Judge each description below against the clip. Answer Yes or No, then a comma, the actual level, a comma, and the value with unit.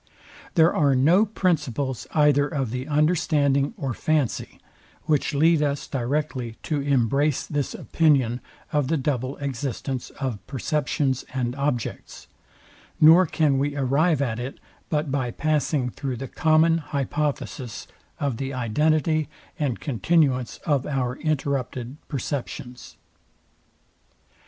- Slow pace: Yes, slow, 120 wpm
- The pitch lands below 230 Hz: Yes, medium, 140 Hz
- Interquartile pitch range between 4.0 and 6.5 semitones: No, average, 2.9 semitones